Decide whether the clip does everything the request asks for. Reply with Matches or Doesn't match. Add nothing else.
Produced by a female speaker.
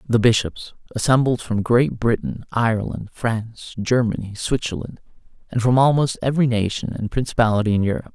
Doesn't match